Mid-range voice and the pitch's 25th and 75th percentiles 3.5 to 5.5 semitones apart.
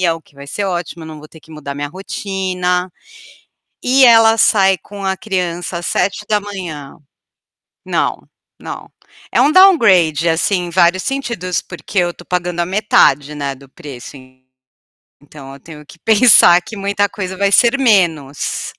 Yes: medium, 180 Hz; average, 4.2 semitones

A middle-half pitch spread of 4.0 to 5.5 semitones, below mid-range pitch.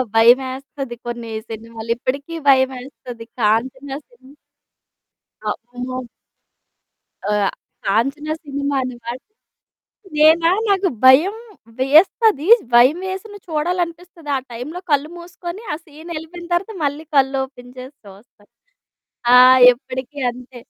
No: average, 4.8 semitones; very high, 275 Hz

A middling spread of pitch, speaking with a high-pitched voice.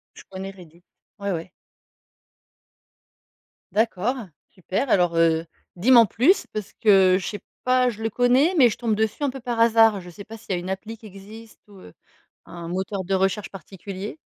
Yes: average, 3.5 semitones; high, 200 Hz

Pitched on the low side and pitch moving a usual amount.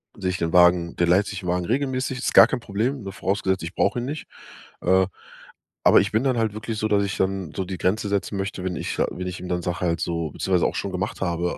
Yes: very low, 95 Hz; average, 3.2 semitones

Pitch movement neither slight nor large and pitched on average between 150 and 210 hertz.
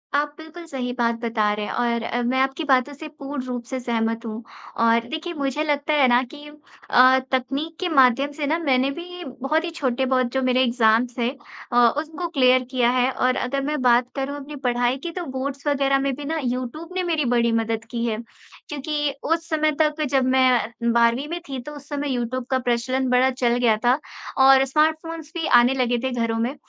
No: average, 3.3 semitones; very high, 265 Hz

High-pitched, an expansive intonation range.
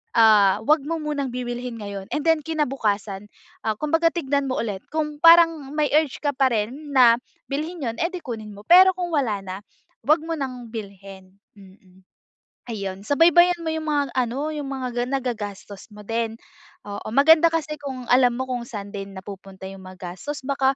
Yes: very high, 255 Hz; wide, 6.5 semitones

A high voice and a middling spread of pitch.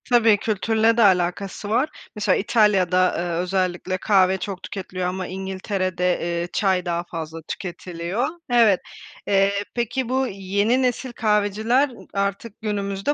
Yes: high, 195 Hz; average, 3.3 semitones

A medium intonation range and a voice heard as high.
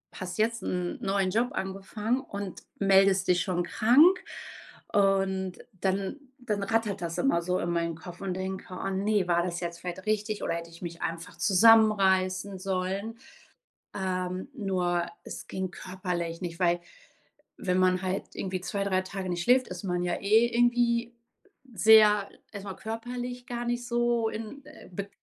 Yes: average, 3.3 semitones; high, 195 Hz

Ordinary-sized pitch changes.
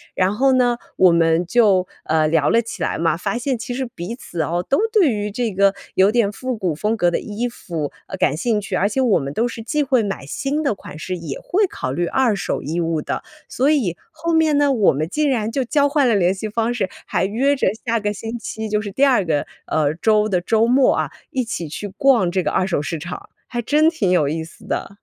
No: wide, 6.3 semitones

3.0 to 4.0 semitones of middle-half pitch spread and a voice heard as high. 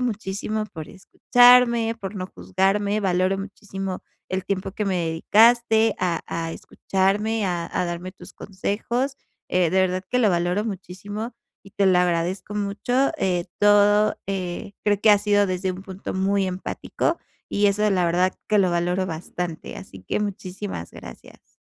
No: narrow, 2.4 semitones; high, 195 Hz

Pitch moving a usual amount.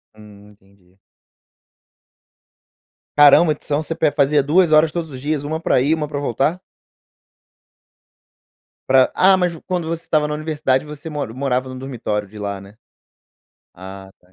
No: wide, 6.4 semitones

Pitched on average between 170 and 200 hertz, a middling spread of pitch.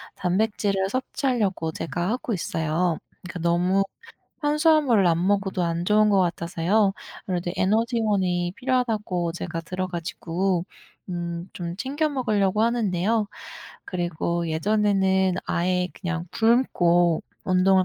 Yes: medium, 185 Hz; average, 3.7 semitones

